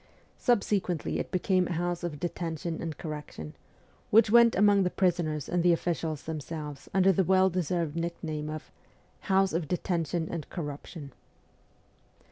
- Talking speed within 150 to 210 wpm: No, average, 140 wpm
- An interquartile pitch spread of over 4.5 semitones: No, average, 3.0 semitones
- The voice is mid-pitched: Yes, medium, 170 Hz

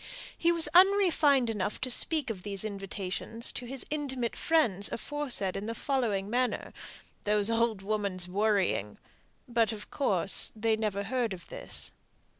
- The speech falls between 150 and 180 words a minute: No, slow, 135 wpm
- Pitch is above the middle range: Yes, high, 220 Hz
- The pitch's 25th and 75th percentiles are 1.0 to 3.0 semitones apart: No, average, 4.6 semitones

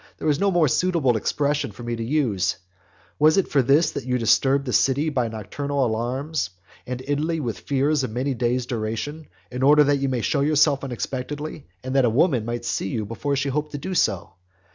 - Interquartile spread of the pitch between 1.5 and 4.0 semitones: Yes, average, 3.7 semitones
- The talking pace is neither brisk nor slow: No, fast, 210 wpm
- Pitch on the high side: No, low, 135 Hz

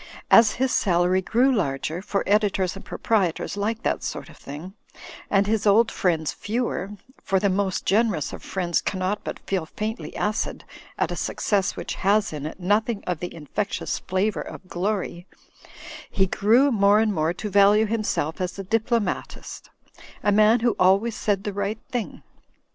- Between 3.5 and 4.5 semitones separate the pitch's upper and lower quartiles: No, average, 2.8 semitones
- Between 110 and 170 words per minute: Yes, average, 165 wpm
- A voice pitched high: Yes, high, 200 Hz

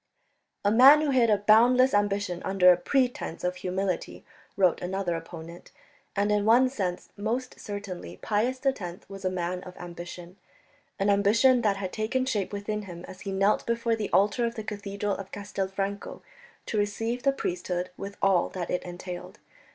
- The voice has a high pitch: Yes, high, 200 Hz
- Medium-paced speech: Yes, average, 170 wpm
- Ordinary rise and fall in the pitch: Yes, average, 3.4 semitones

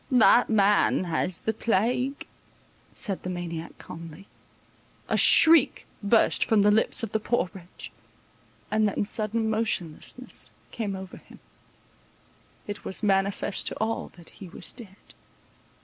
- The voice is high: Yes, high, 205 Hz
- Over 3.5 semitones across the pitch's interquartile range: No, average, 3.1 semitones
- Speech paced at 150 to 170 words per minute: No, slow, 135 wpm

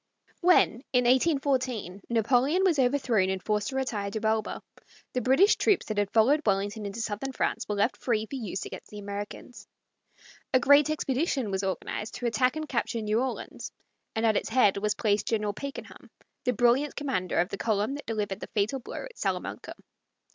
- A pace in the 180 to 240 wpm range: Yes, average, 185 wpm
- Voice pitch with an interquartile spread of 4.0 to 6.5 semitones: Yes, average, 4.4 semitones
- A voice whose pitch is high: Yes, high, 230 Hz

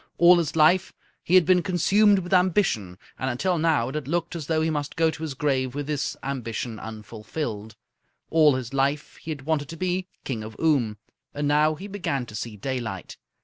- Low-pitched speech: No, medium, 150 Hz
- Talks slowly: No, average, 200 wpm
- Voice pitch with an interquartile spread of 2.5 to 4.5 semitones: No, average, 4.9 semitones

